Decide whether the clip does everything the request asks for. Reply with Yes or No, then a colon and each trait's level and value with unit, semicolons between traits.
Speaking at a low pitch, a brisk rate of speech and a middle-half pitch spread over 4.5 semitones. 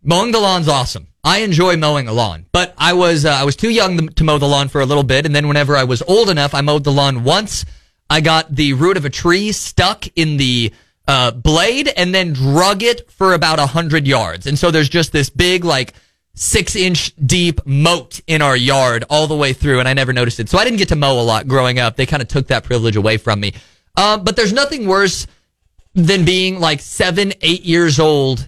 No: medium, 150 Hz; fast, 235 wpm; average, 5.1 semitones